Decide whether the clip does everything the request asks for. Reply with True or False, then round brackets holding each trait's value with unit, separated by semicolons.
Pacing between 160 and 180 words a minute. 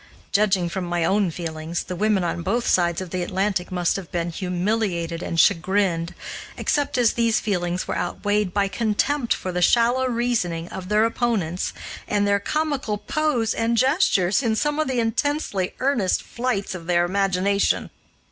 True (165 wpm)